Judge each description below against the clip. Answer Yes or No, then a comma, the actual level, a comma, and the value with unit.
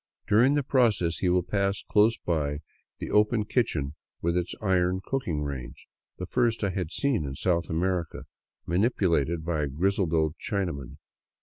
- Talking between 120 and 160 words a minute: No, average, 170 wpm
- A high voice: No, very low, 90 Hz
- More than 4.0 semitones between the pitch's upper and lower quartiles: Yes, average, 4.7 semitones